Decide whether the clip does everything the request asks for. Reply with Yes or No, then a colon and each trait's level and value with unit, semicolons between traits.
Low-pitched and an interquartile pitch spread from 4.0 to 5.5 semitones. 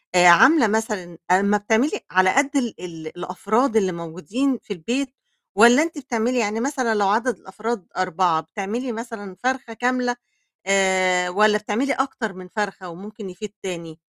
No: high, 210 Hz; average, 4.7 semitones